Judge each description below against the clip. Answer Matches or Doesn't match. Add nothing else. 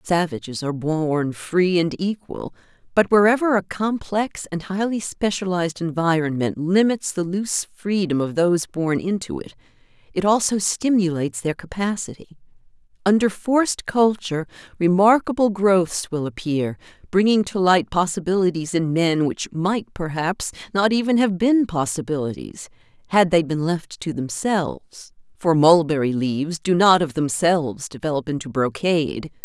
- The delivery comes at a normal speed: Doesn't match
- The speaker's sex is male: Doesn't match